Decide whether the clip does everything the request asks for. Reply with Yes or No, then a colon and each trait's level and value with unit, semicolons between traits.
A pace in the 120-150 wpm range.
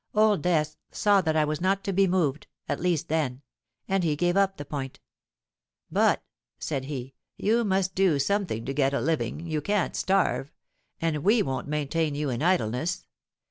No: average, 175 wpm